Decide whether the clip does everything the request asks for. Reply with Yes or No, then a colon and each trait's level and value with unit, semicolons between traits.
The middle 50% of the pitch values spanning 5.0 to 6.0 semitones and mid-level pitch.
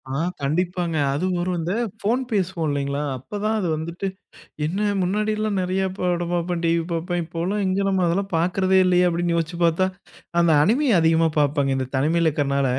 No: average, 2.7 semitones; medium, 175 Hz